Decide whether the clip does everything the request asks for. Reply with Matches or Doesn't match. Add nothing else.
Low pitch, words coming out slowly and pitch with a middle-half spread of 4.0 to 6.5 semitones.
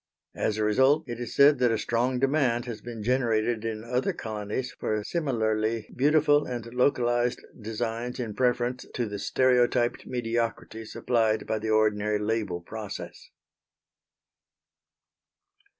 Doesn't match